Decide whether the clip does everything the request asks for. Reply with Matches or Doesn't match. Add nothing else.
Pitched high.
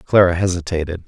Doesn't match